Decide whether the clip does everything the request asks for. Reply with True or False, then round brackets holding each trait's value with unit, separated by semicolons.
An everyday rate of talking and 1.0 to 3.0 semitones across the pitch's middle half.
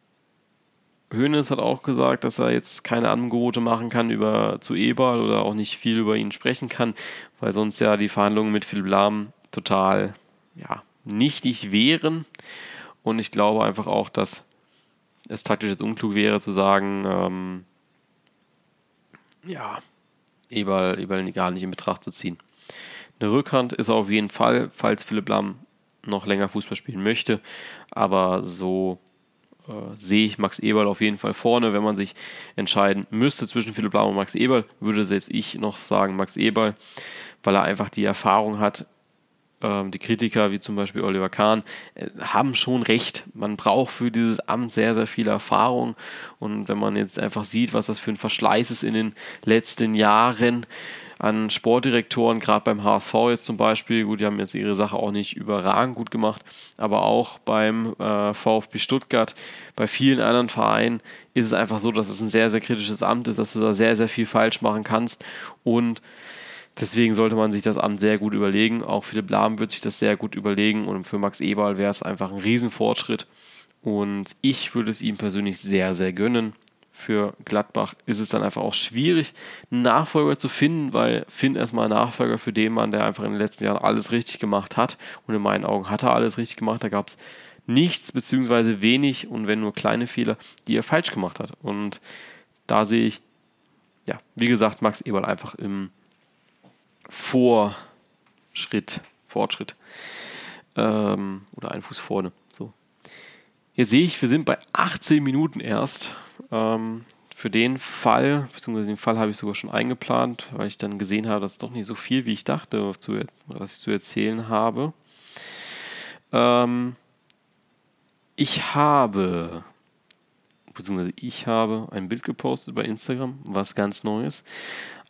True (170 wpm; 2.5 semitones)